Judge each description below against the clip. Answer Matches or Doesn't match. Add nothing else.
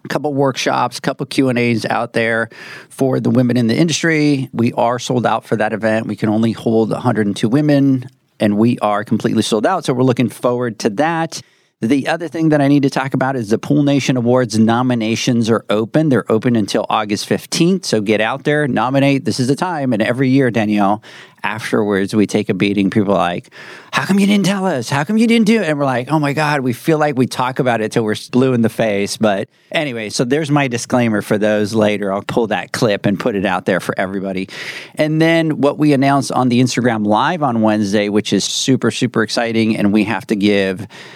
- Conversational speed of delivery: Doesn't match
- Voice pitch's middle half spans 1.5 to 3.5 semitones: Doesn't match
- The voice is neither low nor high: Doesn't match